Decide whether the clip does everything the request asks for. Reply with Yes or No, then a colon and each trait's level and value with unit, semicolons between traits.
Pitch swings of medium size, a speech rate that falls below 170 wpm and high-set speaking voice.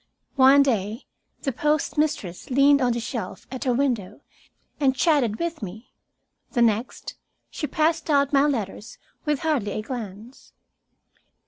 Yes: average, 4.6 semitones; slow, 135 wpm; very high, 260 Hz